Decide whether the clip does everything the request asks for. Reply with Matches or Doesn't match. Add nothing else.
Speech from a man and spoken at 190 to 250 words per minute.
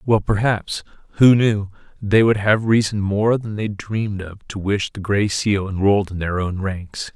Matches